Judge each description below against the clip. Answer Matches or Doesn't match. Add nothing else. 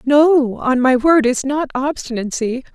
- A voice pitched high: Matches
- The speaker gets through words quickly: Doesn't match